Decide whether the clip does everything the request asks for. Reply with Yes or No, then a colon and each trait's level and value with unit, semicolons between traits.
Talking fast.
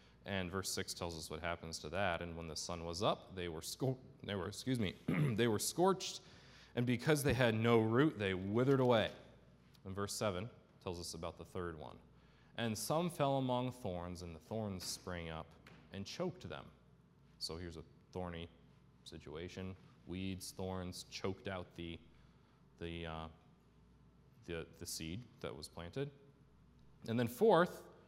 No: average, 165 wpm